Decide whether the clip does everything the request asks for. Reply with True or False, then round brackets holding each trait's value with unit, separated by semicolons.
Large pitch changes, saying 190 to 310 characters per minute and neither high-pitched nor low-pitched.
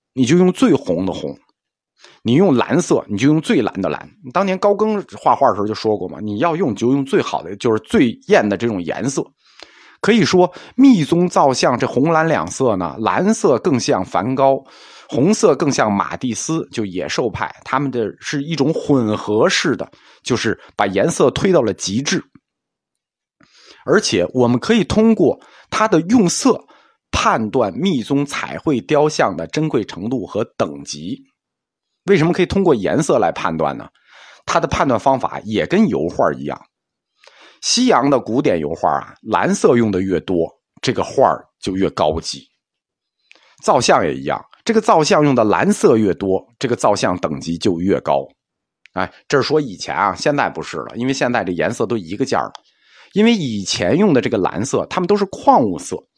True (8.5 semitones; 255 characters per minute; 155 Hz)